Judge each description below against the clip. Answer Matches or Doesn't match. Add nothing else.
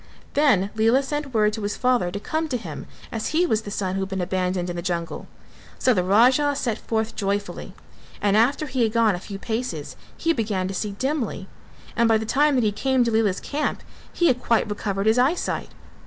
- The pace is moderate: Doesn't match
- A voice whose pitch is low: Doesn't match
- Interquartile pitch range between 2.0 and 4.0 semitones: Doesn't match